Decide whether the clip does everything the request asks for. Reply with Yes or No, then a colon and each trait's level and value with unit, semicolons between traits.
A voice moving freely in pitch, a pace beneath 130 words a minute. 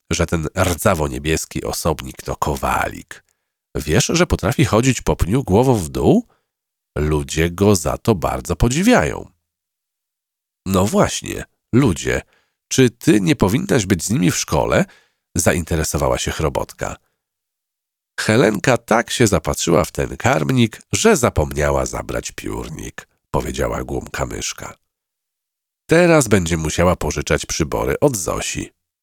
Yes: wide, 6.4 semitones; average, 120 wpm